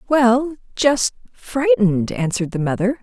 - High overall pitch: Yes, high, 235 Hz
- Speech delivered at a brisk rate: No, slow, 100 wpm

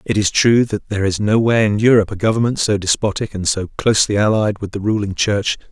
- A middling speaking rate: No, fast, 220 wpm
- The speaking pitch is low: Yes, low, 105 Hz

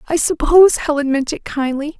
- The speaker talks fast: No, average, 180 wpm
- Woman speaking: Yes, female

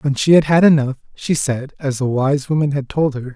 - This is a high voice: No, medium, 140 Hz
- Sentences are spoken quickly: Yes, fast, 270 wpm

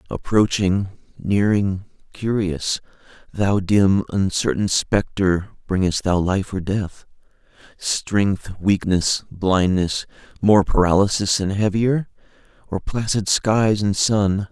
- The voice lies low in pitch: Yes, low, 100 Hz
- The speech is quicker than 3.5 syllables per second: No, 3.4 syllables/s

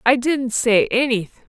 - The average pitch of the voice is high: Yes, high, 245 Hz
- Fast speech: No, average, 155 wpm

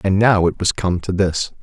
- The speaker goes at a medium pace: No, fast, 260 wpm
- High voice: No, very low, 95 Hz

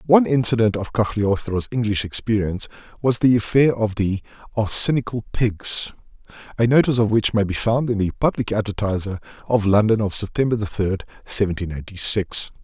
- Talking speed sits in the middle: Yes, average, 145 wpm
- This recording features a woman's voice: No, male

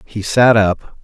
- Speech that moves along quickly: No, average, 175 wpm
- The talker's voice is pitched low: Yes, low, 110 Hz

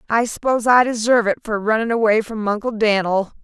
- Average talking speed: Yes, average, 190 wpm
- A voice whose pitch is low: No, high, 220 Hz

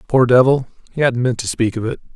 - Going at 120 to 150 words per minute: No, fast, 225 wpm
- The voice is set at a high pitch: No, low, 125 Hz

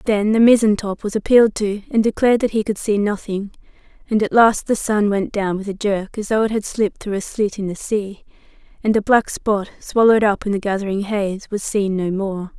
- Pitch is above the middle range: Yes, high, 210 Hz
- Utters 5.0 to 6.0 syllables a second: Yes, 5.4 syllables/s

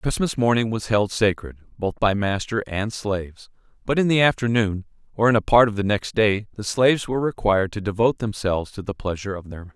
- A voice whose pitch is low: Yes, low, 105 Hz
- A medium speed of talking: No, fast, 215 wpm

